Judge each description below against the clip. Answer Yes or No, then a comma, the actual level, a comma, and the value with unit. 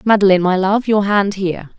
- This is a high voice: Yes, high, 195 Hz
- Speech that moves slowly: No, average, 200 wpm